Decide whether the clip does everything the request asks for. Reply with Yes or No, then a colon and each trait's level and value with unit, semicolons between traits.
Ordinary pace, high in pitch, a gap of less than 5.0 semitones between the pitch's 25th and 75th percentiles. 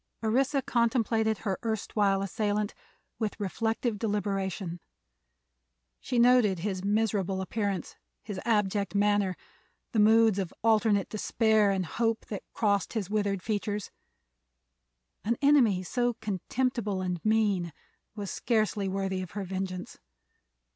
No: slow, 115 wpm; high, 210 Hz; narrow, 2.4 semitones